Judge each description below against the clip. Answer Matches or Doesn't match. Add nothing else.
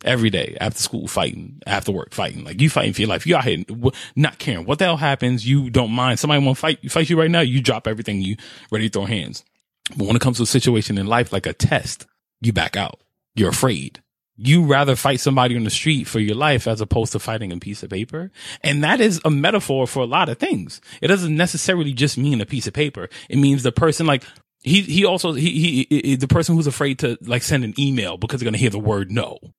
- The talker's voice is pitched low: Matches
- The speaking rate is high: Matches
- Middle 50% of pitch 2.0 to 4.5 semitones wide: Doesn't match